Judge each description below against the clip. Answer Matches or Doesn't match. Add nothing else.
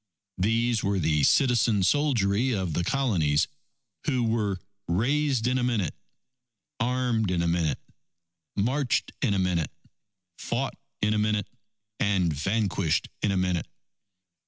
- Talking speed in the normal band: Doesn't match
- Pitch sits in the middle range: Doesn't match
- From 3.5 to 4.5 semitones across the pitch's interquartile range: Doesn't match